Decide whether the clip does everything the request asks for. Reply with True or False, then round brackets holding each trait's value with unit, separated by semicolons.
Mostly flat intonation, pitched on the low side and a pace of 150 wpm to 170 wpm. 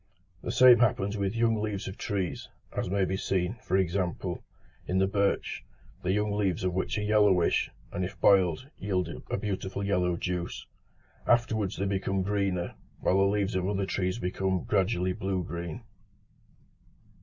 True (2.1 semitones; 95 Hz; 160 wpm)